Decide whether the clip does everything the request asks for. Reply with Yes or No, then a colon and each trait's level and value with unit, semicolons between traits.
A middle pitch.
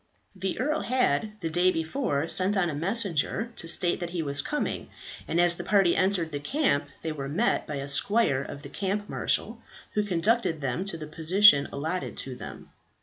Yes: medium, 175 Hz